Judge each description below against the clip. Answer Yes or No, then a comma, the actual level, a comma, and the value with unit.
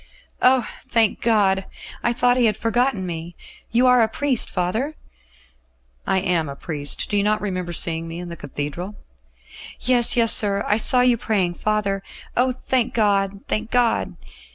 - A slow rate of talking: No, average, 165 wpm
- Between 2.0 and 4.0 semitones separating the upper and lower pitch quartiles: No, average, 4.8 semitones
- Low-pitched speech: No, high, 210 Hz